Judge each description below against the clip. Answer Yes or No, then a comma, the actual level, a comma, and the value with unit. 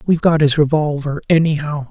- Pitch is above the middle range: No, medium, 150 Hz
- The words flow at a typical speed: Yes, average, 160 wpm